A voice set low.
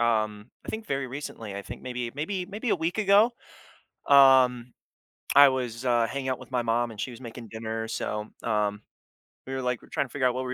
Yes: low, 125 Hz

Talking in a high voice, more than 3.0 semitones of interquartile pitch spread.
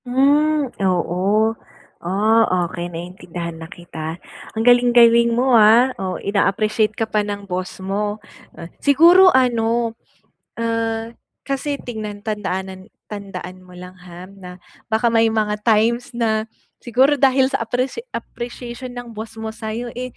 Yes: high, 220 Hz; average, 4.1 semitones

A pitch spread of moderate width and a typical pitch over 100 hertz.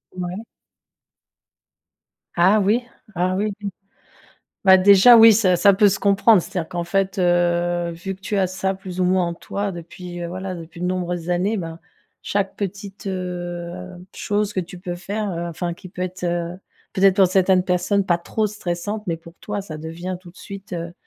No: narrow, 2.1 semitones; medium, 185 Hz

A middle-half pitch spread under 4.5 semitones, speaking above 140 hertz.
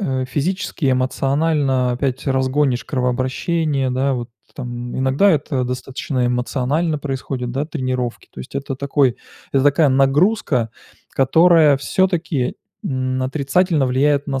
No: narrow, 2.6 semitones; low, 135 Hz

